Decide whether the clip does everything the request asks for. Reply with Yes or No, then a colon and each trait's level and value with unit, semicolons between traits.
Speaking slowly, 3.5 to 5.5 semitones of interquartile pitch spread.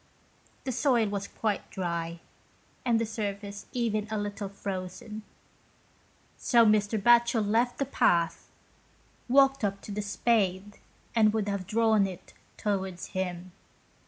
No: slow, 130 wpm; average, 2.7 semitones